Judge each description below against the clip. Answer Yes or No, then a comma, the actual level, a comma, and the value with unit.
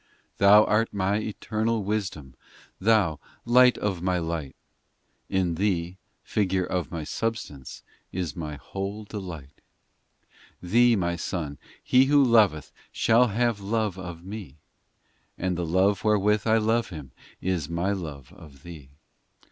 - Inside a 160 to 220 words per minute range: No, average, 140 wpm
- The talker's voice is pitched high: No, very low, 95 Hz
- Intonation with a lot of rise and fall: No, average, 4.3 semitones